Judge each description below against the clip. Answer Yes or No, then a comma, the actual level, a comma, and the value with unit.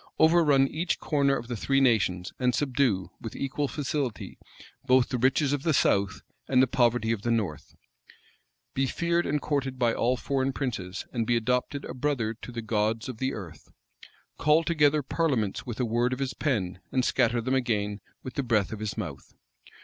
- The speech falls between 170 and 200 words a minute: Yes, average, 190 wpm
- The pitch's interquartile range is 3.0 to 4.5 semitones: Yes, average, 3.7 semitones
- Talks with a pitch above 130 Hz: No, low, 125 Hz